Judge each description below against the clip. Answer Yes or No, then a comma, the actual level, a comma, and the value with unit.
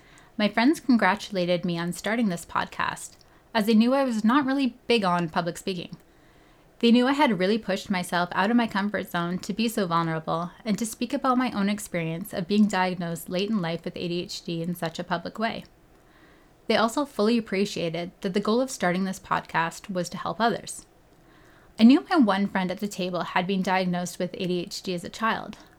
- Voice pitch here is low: No, high, 190 Hz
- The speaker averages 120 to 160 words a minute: No, average, 200 wpm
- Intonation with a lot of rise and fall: No, average, 4.2 semitones